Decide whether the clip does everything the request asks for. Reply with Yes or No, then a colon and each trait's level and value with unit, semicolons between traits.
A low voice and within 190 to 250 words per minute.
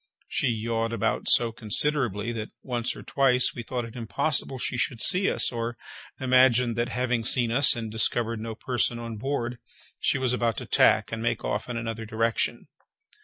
No: low, 120 Hz; average, 180 wpm